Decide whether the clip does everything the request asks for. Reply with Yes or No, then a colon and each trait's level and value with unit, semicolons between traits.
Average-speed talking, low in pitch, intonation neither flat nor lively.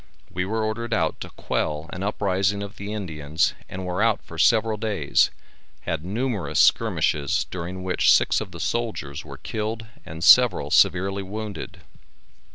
Yes: average, 155 wpm; very low, 95 Hz; average, 4.3 semitones